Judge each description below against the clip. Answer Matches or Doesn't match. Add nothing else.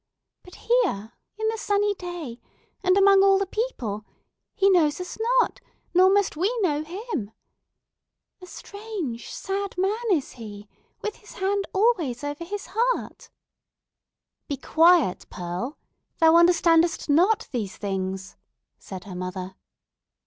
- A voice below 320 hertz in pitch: Doesn't match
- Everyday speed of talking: Doesn't match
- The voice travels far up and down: Matches